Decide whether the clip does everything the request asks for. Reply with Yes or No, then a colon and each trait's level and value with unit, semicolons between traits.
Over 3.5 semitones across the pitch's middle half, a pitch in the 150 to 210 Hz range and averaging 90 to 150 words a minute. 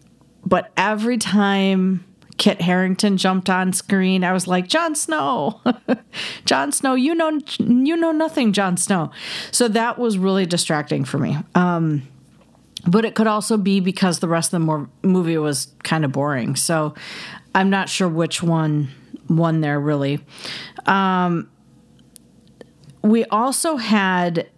Yes: average, 4.8 semitones; medium, 185 Hz; average, 140 wpm